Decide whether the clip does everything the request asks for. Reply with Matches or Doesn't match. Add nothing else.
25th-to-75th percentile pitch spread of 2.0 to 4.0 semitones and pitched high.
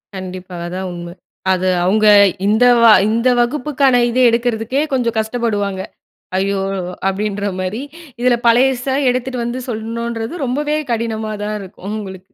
Matches